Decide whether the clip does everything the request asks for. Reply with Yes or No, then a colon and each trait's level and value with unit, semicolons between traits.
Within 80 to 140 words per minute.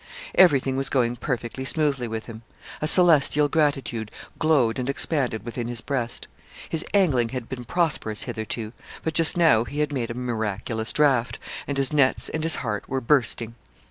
No: average, 170 wpm